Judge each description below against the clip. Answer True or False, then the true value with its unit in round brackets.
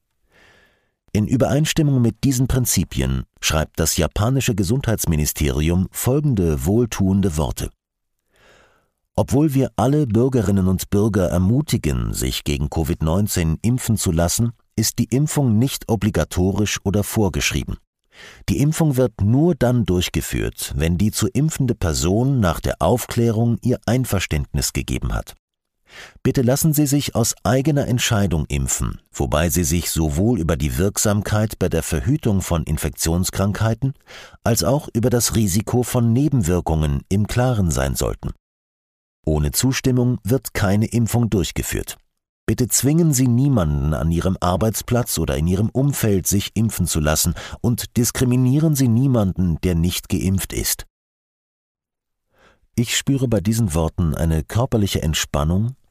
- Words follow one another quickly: False (125 wpm)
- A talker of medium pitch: False (105 Hz)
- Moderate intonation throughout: False (6.8 semitones)